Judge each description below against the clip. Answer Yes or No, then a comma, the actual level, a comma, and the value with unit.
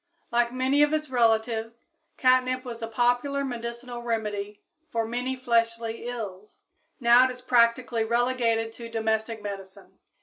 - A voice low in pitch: No, high, 235 Hz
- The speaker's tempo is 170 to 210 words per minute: No, slow, 135 wpm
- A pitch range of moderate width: No, narrow, 2.0 semitones